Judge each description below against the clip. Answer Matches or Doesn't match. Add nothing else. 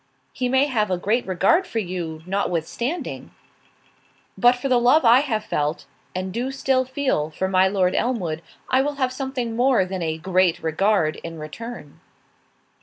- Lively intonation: Matches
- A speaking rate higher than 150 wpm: Matches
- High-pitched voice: Matches